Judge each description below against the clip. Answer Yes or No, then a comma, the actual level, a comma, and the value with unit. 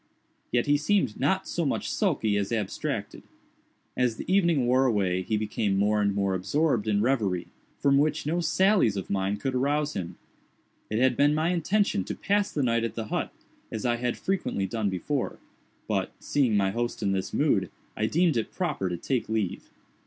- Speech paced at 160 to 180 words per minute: No, average, 190 wpm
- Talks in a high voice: No, low, 120 Hz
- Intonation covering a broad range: Yes, wide, 6.2 semitones